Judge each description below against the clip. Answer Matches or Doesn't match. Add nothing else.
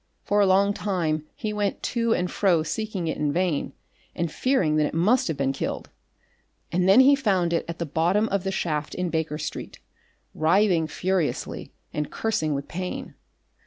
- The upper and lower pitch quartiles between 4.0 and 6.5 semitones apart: Matches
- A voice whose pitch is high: Doesn't match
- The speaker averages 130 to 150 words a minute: Doesn't match